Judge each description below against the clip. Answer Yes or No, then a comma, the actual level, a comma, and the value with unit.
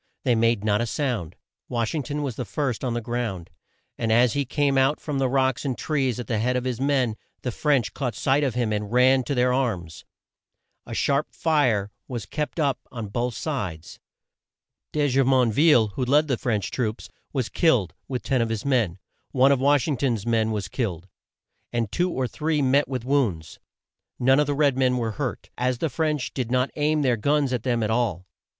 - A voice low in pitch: Yes, low, 125 Hz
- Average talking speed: No, fast, 210 wpm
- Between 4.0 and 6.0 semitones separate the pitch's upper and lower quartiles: No, average, 3.6 semitones